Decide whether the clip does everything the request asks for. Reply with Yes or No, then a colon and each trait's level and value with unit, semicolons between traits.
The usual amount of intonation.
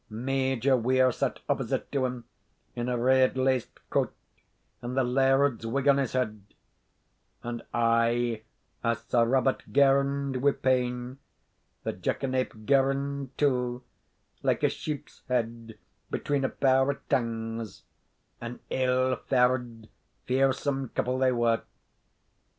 No: narrow, 2.1 semitones